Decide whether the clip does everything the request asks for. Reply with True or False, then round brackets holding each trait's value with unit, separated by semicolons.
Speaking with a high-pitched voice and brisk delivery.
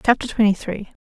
False (210 Hz; 175 wpm)